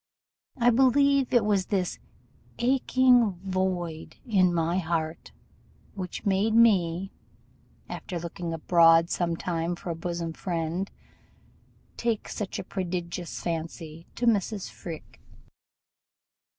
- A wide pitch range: No, average, 4.1 semitones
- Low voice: No, medium, 180 Hz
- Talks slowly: Yes, slow, 110 wpm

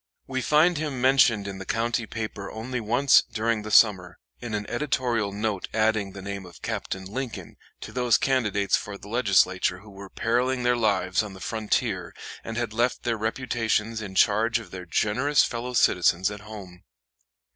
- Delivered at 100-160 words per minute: No, average, 175 wpm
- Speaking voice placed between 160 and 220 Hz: No, low, 110 Hz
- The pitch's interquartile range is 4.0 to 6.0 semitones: No, average, 3.4 semitones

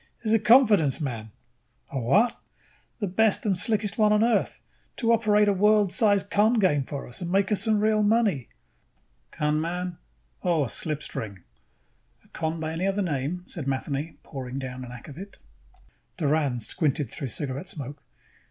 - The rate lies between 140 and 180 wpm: Yes, average, 160 wpm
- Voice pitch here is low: No, medium, 175 Hz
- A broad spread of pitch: Yes, wide, 6.9 semitones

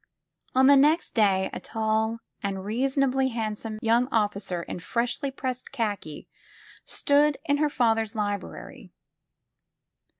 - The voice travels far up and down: No, average, 4.2 semitones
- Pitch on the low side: No, high, 230 Hz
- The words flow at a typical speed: No, slow, 120 wpm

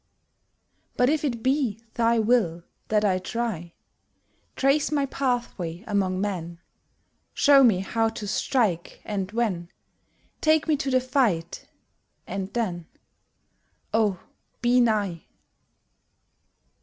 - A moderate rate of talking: No, slow, 110 wpm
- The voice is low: No, high, 220 Hz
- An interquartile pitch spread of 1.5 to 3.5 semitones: No, average, 5.2 semitones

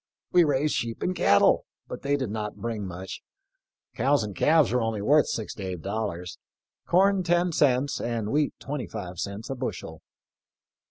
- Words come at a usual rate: Yes, average, 170 wpm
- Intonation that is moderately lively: No, wide, 6.1 semitones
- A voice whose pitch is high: No, low, 115 Hz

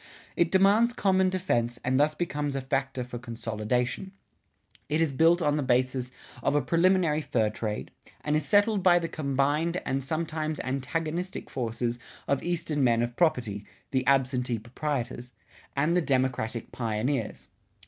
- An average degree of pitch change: Yes, average, 5.0 semitones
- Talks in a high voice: No, medium, 140 Hz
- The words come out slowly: No, average, 150 wpm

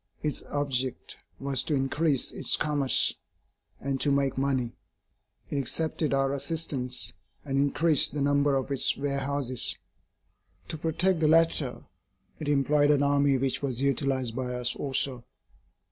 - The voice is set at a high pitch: No, medium, 140 Hz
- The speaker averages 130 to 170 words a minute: Yes, slow, 135 wpm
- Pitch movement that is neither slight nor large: No, narrow, 1.6 semitones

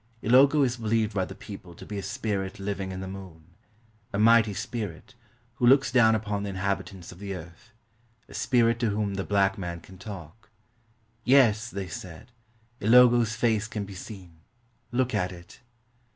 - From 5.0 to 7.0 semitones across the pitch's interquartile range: No, average, 3.3 semitones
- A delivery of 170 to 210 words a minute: Yes, average, 180 wpm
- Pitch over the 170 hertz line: No, low, 105 Hz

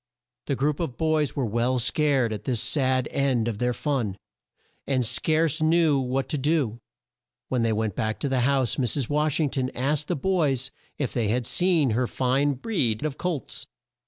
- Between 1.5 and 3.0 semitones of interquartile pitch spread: No, average, 3.6 semitones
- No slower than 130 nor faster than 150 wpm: No, average, 185 wpm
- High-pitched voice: No, low, 135 Hz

